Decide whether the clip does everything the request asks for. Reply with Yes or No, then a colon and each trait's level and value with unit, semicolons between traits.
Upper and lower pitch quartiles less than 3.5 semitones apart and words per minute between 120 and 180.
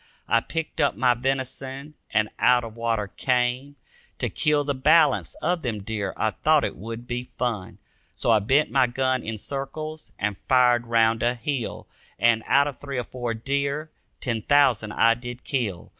Yes: average, 3.1 semitones; average, 175 wpm